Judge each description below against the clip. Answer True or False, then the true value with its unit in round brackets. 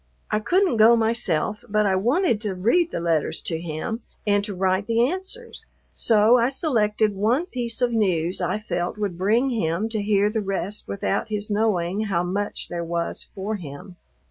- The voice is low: False (210 Hz)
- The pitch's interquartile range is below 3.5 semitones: False (3.9 semitones)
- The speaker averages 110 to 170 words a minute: False (180 wpm)